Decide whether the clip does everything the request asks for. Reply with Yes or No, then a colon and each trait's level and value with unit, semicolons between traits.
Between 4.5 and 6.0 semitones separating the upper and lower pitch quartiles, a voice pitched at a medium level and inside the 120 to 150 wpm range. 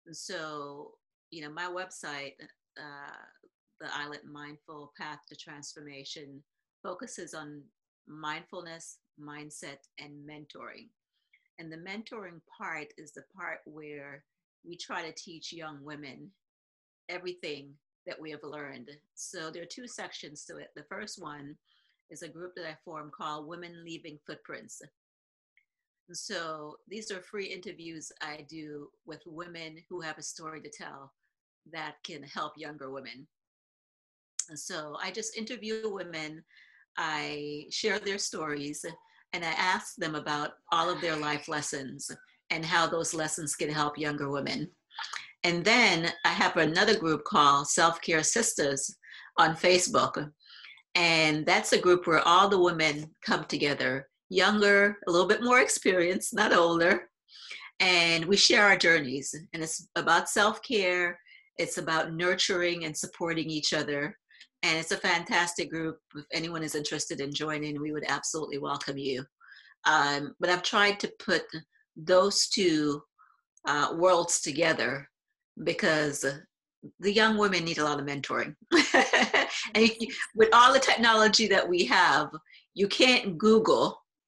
No: average, 3.7 semitones; medium, 160 Hz; average, 140 wpm